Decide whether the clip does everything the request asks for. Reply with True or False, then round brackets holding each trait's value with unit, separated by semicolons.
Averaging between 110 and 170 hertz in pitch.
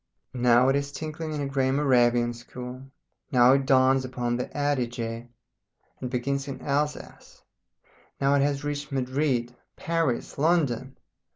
True (135 Hz)